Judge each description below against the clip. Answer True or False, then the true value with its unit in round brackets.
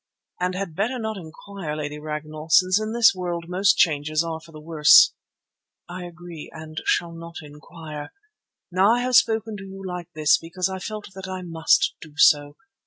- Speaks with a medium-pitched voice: True (175 Hz)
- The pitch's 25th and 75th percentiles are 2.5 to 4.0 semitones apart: True (3.6 semitones)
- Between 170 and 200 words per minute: True (180 wpm)